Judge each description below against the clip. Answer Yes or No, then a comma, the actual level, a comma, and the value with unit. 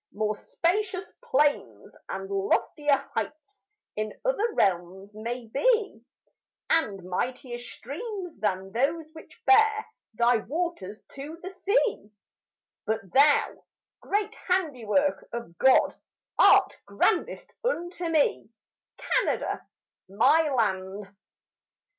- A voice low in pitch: No, very high, 275 Hz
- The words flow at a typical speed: No, slow, 100 wpm